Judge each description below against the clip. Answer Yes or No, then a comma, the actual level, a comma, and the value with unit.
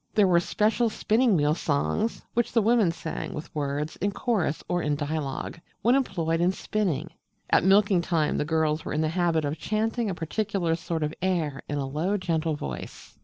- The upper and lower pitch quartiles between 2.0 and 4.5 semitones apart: No, average, 5.0 semitones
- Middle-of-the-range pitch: Yes, medium, 170 Hz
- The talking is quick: No, average, 190 wpm